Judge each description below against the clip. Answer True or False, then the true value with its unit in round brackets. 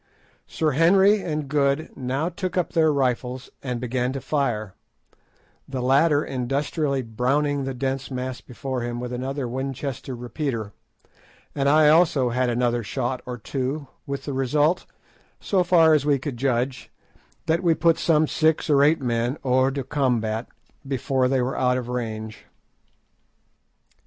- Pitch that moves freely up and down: False (3.2 semitones)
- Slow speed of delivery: False (150 wpm)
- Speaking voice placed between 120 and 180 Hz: True (135 Hz)